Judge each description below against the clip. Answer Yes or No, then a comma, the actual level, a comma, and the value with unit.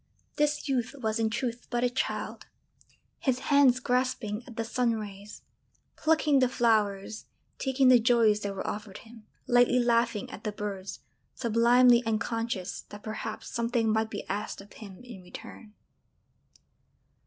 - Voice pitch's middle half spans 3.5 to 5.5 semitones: No, average, 2.7 semitones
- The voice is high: Yes, high, 230 Hz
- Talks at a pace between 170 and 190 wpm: No, average, 150 wpm